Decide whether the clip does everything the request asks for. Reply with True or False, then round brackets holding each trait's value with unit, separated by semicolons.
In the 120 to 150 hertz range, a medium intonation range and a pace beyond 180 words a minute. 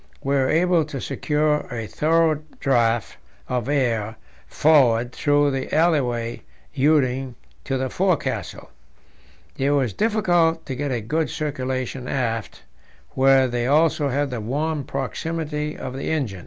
False (135 Hz; 3.5 semitones; 135 wpm)